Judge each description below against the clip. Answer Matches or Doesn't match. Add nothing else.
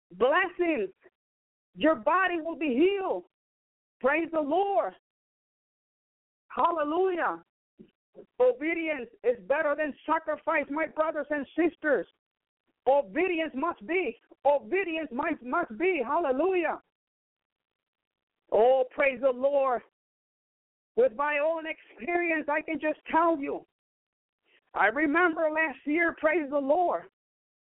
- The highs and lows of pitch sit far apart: Doesn't match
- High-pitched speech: Matches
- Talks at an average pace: Doesn't match